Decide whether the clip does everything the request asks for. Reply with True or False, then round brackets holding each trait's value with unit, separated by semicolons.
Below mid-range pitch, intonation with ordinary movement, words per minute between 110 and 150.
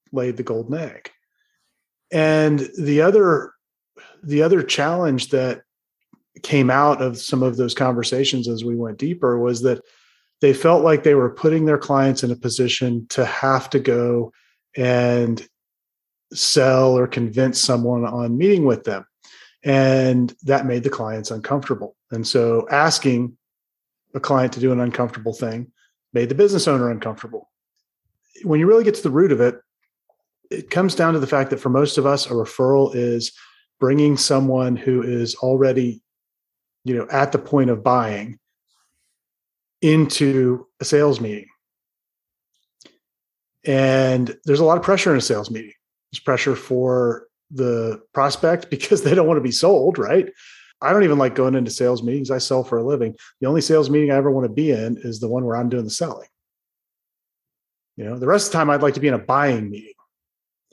False (130 Hz; 3.2 semitones; 175 wpm)